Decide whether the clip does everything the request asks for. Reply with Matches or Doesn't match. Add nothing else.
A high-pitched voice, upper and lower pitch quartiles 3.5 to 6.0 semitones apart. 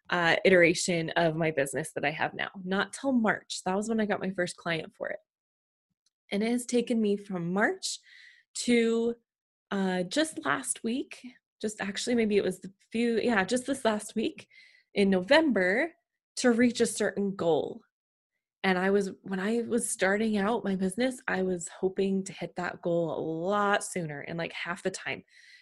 Matches